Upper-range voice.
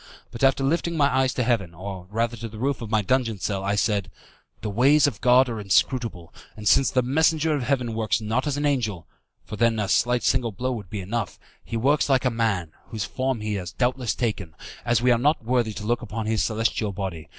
No: low, 115 Hz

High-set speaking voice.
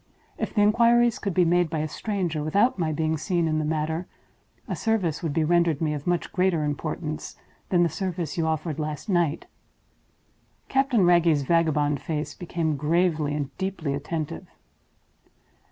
No: medium, 165 Hz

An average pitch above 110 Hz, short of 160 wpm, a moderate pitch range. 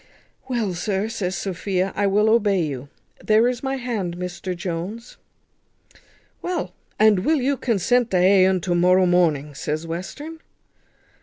Yes: high, 190 Hz; average, 145 wpm; average, 4.4 semitones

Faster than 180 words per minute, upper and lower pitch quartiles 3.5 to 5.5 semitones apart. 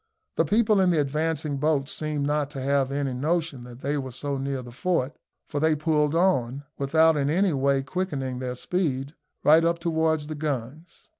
No: average, 190 wpm; average, 3.0 semitones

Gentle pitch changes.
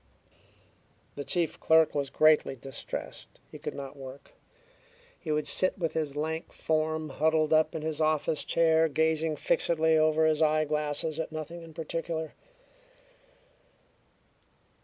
Yes: narrow, 1.0 semitones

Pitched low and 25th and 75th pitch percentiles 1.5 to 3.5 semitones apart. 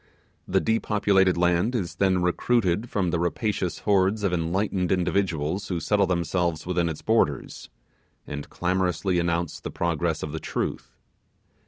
Yes: very low, 90 Hz; narrow, 2.6 semitones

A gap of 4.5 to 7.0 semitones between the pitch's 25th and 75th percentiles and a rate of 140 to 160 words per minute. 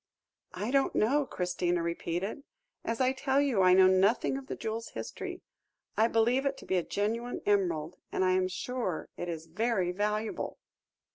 No: average, 5.0 semitones; average, 170 wpm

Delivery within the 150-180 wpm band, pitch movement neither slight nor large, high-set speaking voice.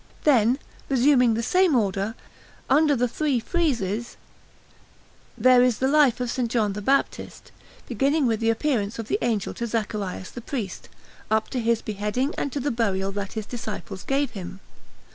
Yes: average, 165 wpm; average, 4.2 semitones; high, 235 Hz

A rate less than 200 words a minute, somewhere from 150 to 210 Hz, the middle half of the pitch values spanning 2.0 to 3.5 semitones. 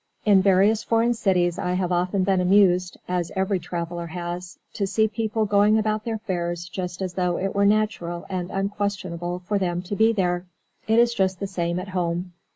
Yes: average, 190 wpm; medium, 185 Hz; narrow, 2.6 semitones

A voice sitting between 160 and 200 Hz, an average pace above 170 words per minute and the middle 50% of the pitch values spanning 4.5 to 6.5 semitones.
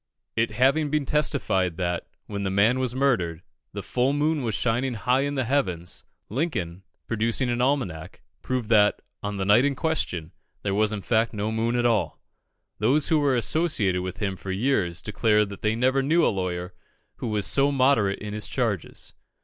No: low, 115 Hz; average, 185 wpm; average, 5.2 semitones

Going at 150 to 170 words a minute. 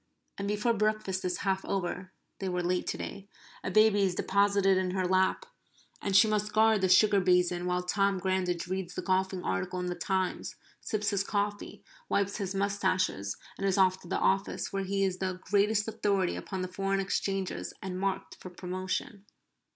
No: average, 180 wpm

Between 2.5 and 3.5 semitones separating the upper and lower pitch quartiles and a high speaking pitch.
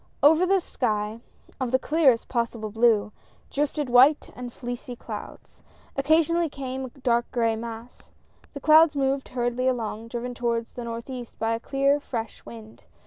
Yes: average, 3.1 semitones; high, 245 Hz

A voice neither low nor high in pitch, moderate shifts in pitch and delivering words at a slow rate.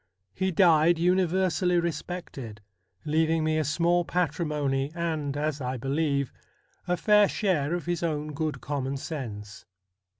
Yes: medium, 155 Hz; average, 3.8 semitones; slow, 130 wpm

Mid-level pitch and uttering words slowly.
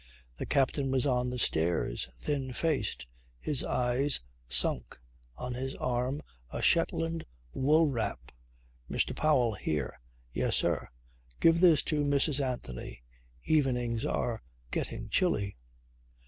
No: low, 130 Hz; slow, 120 wpm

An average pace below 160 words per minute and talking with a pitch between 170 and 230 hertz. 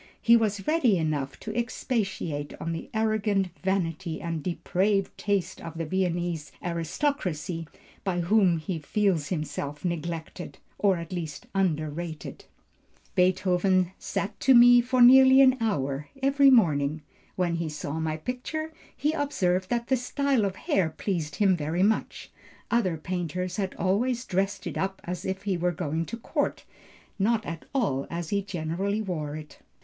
Yes: average, 150 wpm; medium, 185 Hz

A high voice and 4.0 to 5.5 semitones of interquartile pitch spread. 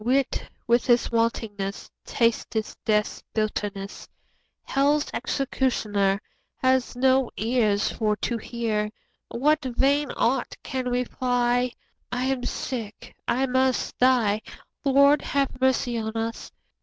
No: high, 245 Hz; average, 3.1 semitones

